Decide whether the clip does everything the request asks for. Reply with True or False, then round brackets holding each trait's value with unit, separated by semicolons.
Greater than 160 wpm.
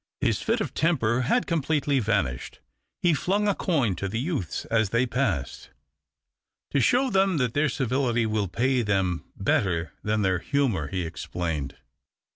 False (155 wpm)